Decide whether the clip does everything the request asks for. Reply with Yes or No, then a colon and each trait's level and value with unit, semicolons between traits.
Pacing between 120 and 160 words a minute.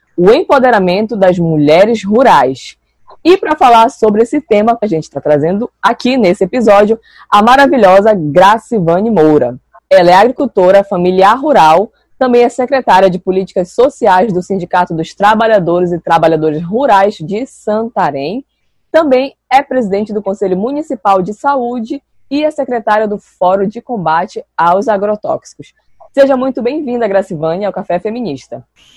Yes: average, 140 wpm